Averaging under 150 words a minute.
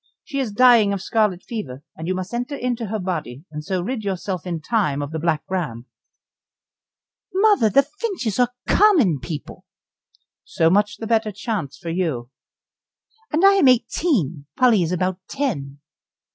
No: average, 160 wpm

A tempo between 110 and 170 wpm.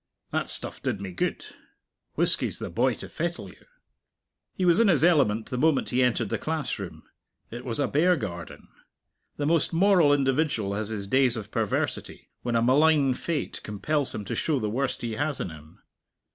No: average, 185 wpm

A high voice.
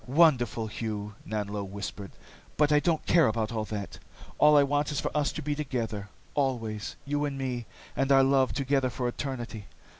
No: low, 130 Hz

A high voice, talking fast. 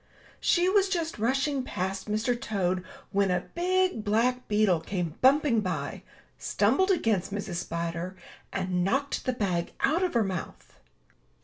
No: high, 215 Hz; average, 140 wpm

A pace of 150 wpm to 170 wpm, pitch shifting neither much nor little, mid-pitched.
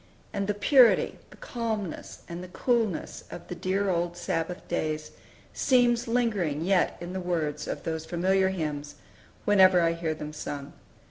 Yes: average, 155 wpm; average, 3.9 semitones; medium, 180 Hz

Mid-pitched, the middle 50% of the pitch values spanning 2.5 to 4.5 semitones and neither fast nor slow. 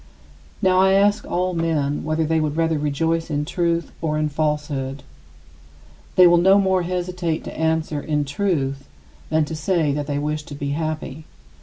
Yes: medium, 160 Hz; average, 2.8 semitones; average, 170 wpm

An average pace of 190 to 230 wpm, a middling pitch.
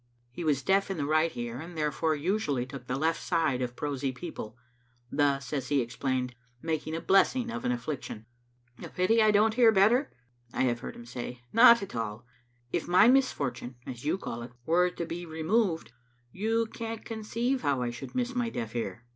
Yes: average, 195 wpm; medium, 160 Hz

